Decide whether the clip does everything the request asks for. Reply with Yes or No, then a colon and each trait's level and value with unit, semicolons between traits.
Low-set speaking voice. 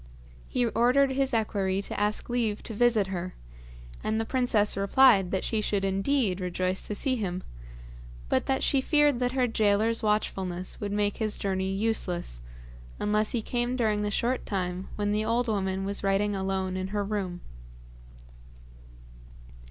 No: high, 210 Hz